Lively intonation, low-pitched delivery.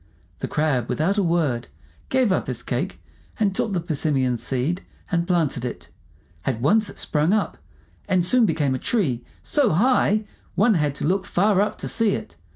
No: wide, 6.4 semitones; medium, 175 Hz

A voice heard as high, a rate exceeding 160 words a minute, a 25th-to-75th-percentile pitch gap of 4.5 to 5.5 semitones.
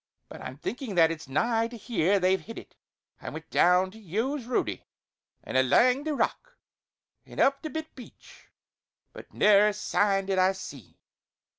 Yes: high, 210 Hz; average, 170 wpm; average, 5.1 semitones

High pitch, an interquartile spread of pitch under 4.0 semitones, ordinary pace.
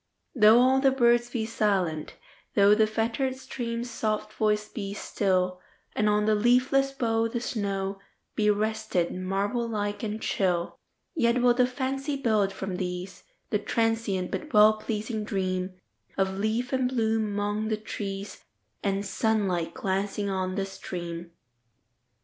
No: high, 215 Hz; average, 3.2 semitones; slow, 120 wpm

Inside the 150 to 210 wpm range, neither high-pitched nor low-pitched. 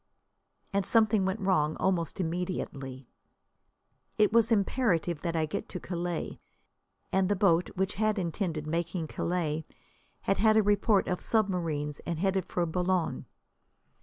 No: slow, 135 wpm; medium, 180 Hz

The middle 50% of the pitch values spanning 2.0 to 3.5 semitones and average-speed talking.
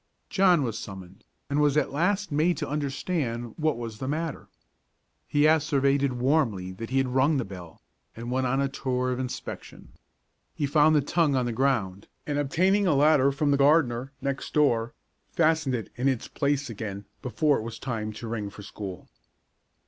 No: average, 4.3 semitones; average, 180 wpm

